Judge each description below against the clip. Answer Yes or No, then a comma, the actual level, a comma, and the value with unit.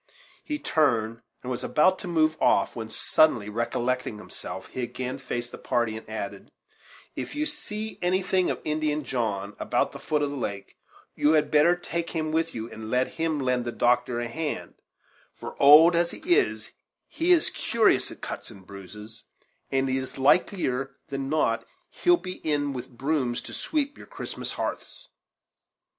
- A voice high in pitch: No, medium, 140 Hz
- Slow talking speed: No, average, 170 wpm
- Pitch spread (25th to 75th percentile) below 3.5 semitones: No, wide, 5.5 semitones